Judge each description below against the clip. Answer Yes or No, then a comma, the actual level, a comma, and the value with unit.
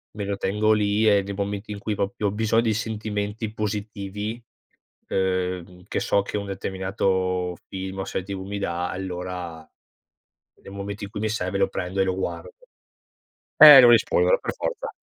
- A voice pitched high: No, low, 100 Hz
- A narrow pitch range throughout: Yes, narrow, 2.1 semitones